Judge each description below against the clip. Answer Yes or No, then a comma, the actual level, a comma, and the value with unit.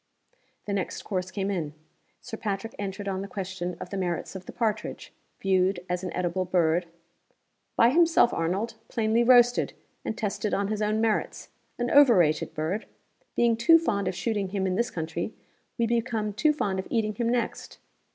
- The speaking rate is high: No, average, 175 wpm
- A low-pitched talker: No, high, 200 Hz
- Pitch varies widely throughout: No, average, 3.7 semitones